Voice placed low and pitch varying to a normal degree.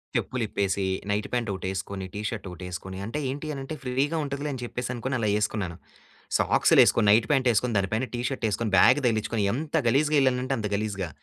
Yes: low, 115 Hz; average, 4.6 semitones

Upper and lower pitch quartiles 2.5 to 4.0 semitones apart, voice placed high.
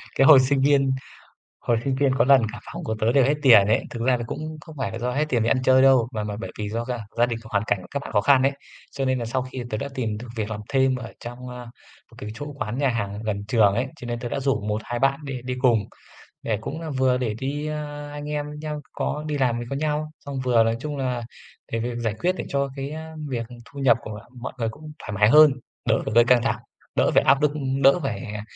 No: average, 3.5 semitones; low, 130 Hz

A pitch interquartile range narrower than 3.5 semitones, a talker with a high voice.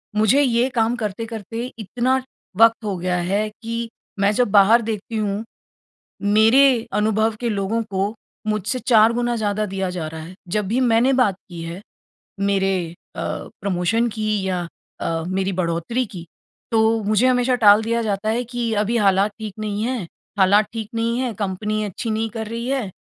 Yes: average, 2.9 semitones; high, 215 Hz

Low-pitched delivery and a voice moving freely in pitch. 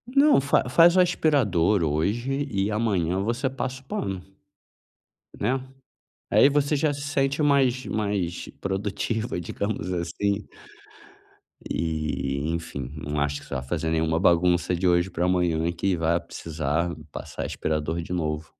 Yes: very low, 90 Hz; wide, 7.2 semitones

